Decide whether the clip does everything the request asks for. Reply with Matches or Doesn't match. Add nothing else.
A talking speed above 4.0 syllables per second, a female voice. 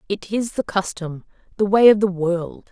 Matches